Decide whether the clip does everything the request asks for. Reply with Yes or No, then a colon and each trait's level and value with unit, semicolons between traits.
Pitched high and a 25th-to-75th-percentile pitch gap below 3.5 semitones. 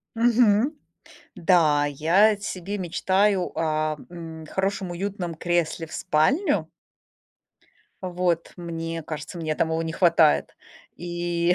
No: medium, 175 Hz; average, 2.9 semitones